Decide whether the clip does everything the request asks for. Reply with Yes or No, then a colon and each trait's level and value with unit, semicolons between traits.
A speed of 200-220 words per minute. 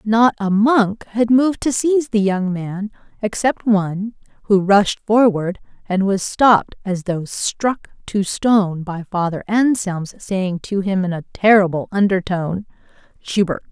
No: average, 150 wpm